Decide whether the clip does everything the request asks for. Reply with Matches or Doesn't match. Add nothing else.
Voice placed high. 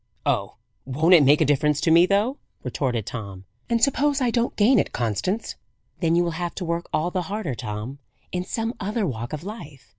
Doesn't match